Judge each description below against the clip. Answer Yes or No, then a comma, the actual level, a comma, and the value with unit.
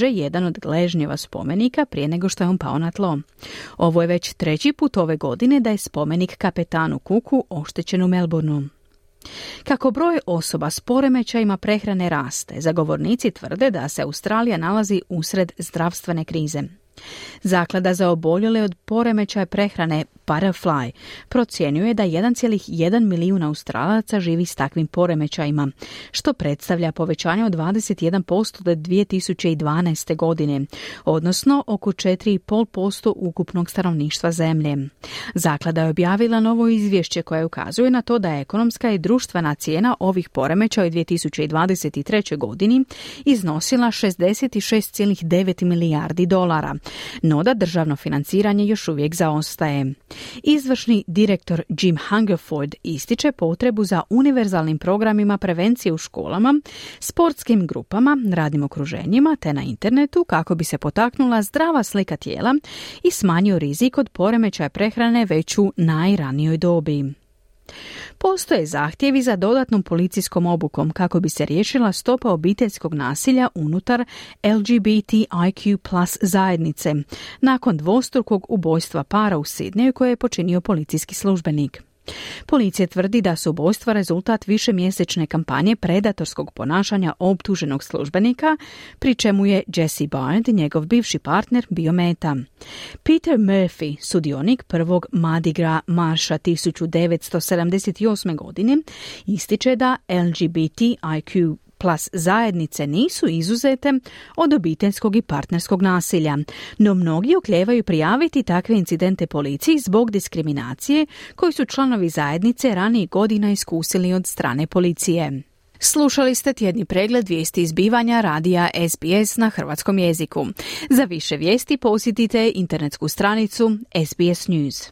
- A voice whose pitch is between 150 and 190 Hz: Yes, medium, 185 Hz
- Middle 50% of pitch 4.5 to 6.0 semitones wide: Yes, wide, 5.4 semitones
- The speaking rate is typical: Yes, average, 120 wpm